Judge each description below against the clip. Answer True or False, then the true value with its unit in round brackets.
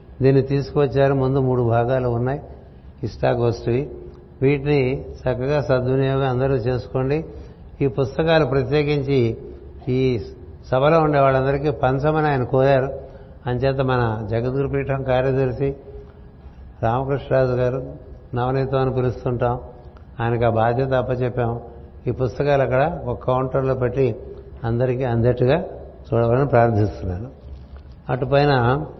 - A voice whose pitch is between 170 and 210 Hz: False (130 Hz)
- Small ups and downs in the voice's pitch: True (2.3 semitones)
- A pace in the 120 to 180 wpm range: False (95 wpm)